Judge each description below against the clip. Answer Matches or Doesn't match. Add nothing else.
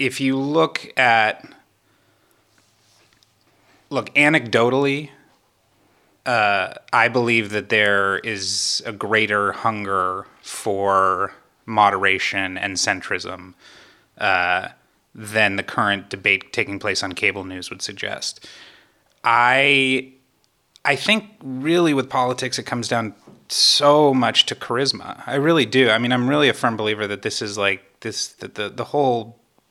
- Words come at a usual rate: Doesn't match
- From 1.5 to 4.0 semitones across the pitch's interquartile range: Doesn't match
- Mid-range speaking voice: Doesn't match